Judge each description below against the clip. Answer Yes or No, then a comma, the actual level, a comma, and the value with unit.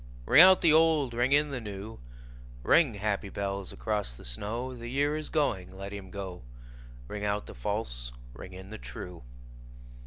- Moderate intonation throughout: No, wide, 5.9 semitones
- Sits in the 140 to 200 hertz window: No, low, 105 Hz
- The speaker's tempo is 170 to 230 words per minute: Yes, average, 175 wpm